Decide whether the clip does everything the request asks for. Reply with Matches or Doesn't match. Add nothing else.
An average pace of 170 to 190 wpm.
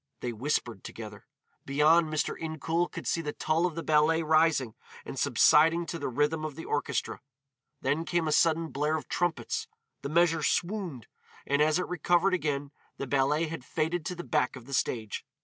Matches